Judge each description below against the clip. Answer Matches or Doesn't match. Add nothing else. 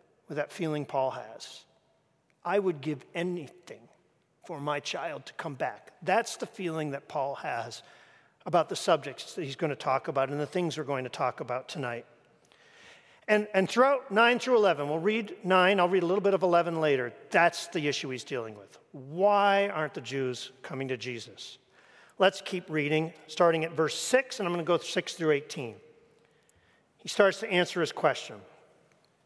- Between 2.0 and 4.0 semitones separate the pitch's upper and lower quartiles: Doesn't match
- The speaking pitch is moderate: Matches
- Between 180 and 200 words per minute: Matches